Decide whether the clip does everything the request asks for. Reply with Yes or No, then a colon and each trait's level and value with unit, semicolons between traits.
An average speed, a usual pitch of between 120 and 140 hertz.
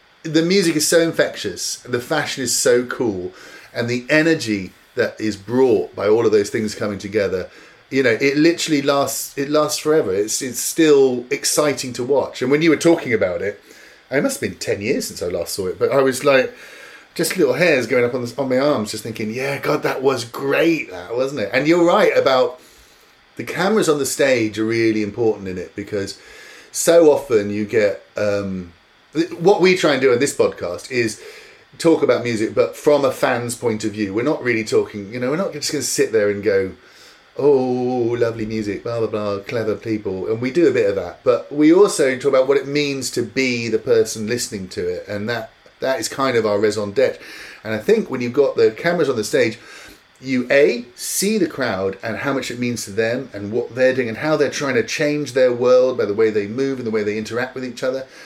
No: fast, 225 wpm; low, 135 Hz